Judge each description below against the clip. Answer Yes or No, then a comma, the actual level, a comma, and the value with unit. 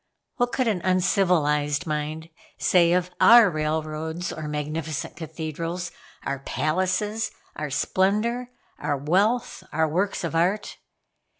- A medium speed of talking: No, slow, 115 wpm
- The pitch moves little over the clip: No, average, 3.9 semitones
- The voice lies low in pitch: No, medium, 170 Hz